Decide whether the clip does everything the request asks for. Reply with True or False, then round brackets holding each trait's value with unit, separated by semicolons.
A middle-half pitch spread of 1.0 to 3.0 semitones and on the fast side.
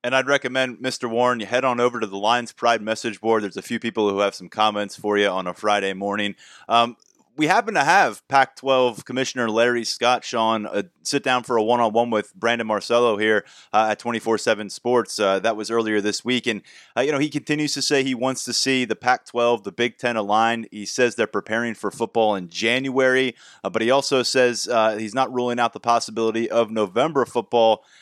True (2.6 semitones; 215 wpm)